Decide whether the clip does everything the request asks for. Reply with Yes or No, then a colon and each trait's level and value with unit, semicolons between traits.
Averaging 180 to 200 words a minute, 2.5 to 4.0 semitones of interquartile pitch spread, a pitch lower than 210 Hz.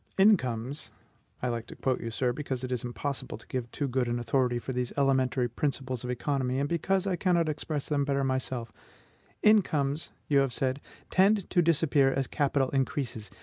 Yes: average, 185 wpm; average, 2.9 semitones; low, 135 Hz